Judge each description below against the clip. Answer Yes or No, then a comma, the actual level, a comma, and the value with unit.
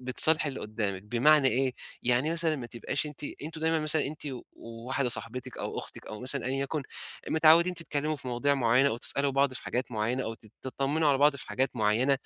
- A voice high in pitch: No, low, 135 Hz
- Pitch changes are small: No, average, 3.7 semitones